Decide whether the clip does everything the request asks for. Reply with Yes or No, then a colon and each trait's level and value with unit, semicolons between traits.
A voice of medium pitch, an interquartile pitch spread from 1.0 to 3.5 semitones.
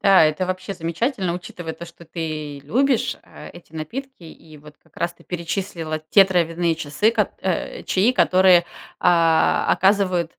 Yes: medium, 175 Hz; average, 2.9 semitones